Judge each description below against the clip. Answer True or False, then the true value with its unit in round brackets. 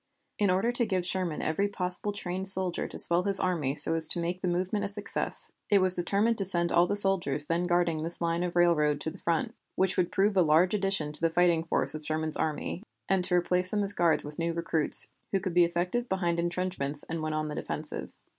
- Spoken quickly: True (230 wpm)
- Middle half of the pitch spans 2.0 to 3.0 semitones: True (2.7 semitones)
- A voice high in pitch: False (175 Hz)